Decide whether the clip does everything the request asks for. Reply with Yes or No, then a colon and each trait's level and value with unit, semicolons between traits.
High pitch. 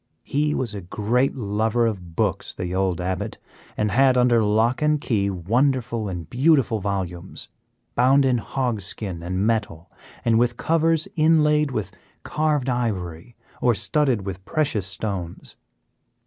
No: low, 115 Hz